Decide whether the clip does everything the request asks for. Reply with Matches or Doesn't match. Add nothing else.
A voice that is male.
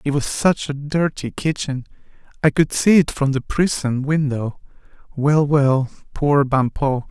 Matches